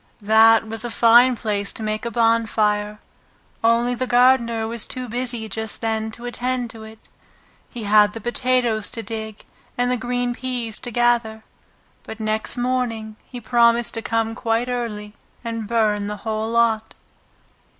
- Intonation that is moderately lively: No, narrow, 1.7 semitones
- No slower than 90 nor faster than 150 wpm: No, average, 160 wpm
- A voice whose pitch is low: No, high, 230 Hz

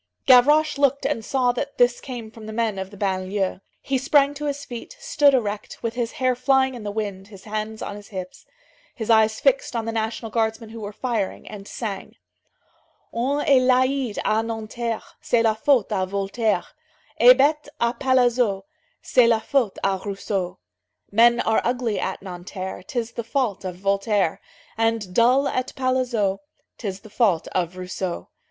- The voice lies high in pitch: Yes, high, 225 Hz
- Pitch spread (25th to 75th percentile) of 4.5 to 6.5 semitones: No, average, 4.0 semitones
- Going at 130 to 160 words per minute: No, average, 175 wpm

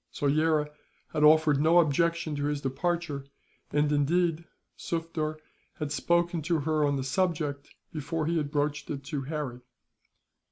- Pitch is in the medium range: Yes, medium, 150 Hz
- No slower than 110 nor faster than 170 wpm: Yes, average, 145 wpm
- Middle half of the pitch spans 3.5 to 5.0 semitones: No, narrow, 2.4 semitones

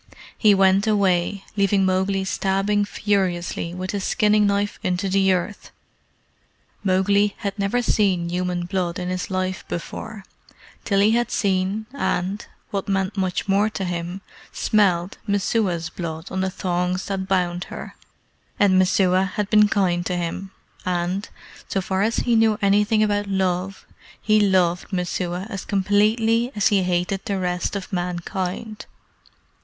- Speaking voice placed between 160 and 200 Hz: Yes, high, 190 Hz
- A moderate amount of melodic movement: No, narrow, 2.1 semitones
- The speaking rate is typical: Yes, average, 145 wpm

